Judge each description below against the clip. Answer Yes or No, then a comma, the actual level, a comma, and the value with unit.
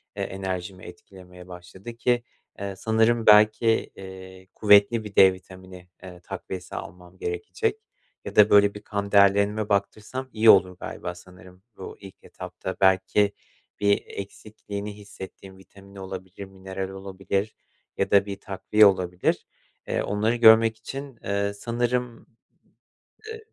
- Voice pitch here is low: Yes, low, 100 Hz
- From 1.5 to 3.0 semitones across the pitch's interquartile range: Yes, narrow, 2.4 semitones